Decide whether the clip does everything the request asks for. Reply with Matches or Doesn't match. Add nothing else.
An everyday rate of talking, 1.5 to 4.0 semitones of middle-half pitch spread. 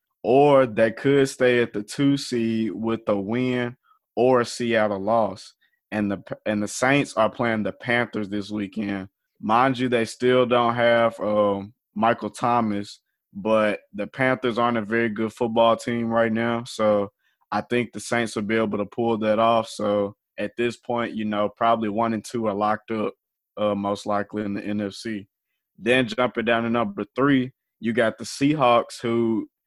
Matches